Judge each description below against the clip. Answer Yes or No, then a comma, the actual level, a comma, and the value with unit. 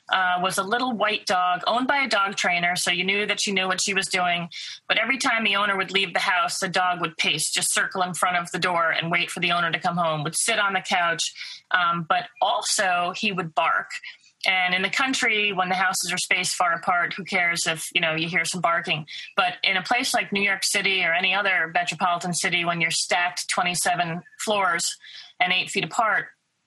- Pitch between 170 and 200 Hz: Yes, medium, 185 Hz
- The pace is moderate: No, fast, 230 wpm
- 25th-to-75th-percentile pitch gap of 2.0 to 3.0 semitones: Yes, average, 2.7 semitones